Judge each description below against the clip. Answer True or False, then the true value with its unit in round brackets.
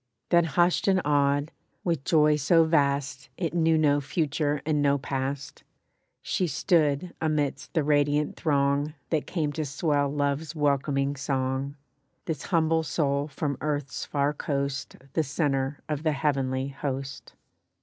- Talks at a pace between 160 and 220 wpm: False (140 wpm)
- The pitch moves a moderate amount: False (2.0 semitones)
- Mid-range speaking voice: True (145 Hz)